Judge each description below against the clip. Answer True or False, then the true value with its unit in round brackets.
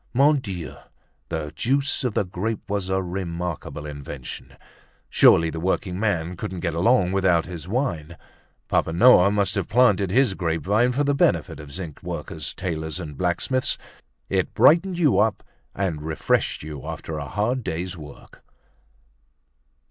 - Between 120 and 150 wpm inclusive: True (145 wpm)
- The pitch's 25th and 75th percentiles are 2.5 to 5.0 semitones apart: False (5.4 semitones)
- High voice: False (95 Hz)